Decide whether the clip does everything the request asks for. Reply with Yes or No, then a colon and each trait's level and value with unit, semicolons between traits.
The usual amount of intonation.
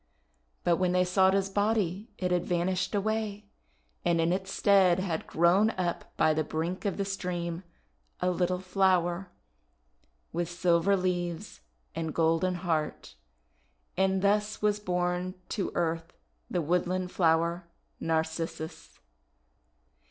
No: narrow, 2.2 semitones